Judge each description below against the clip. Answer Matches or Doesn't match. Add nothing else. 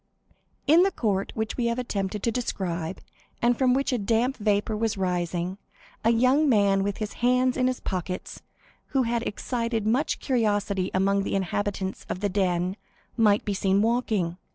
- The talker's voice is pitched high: Matches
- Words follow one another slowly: Doesn't match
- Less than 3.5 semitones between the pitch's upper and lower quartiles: Doesn't match